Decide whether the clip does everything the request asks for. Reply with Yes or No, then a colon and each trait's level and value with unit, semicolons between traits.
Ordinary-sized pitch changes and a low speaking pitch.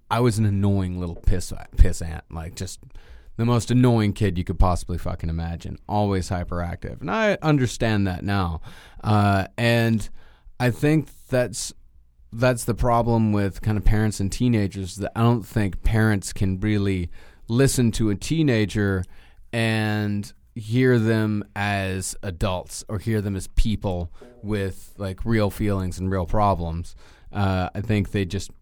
Yes: average, 3.6 semitones; low, 100 Hz